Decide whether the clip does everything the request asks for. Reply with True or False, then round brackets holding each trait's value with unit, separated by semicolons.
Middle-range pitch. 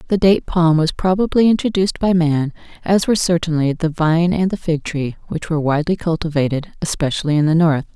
True (165 Hz)